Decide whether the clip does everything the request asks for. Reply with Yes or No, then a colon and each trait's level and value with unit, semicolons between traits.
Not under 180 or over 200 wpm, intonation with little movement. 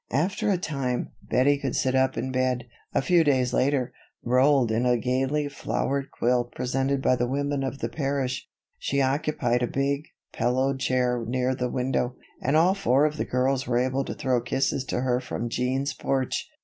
Yes: average, 185 wpm; narrow, 1.9 semitones